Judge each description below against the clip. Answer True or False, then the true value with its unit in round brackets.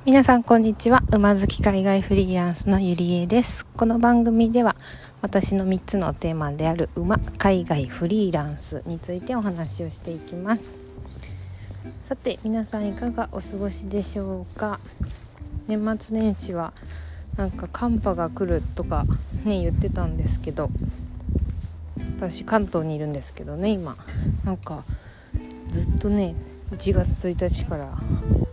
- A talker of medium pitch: True (170 Hz)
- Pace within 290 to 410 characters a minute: False (270 characters per minute)